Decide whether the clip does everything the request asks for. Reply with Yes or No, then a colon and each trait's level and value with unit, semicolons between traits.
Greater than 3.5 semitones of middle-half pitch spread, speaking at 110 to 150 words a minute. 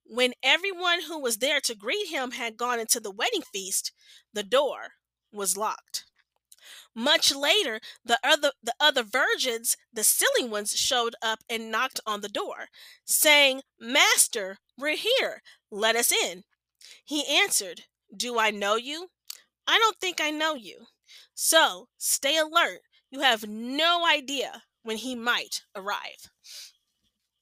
Yes: wide, 5.6 semitones; average, 140 wpm